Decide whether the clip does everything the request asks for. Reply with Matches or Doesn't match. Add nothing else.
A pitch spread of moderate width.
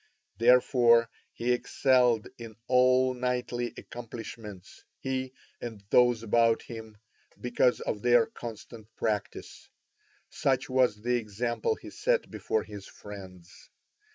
Doesn't match